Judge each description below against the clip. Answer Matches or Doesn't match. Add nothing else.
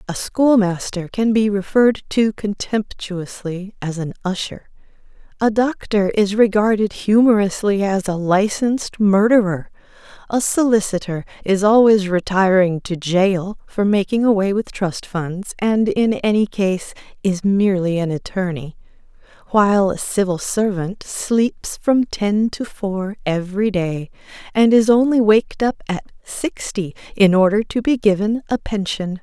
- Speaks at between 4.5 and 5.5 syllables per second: Doesn't match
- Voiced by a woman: Matches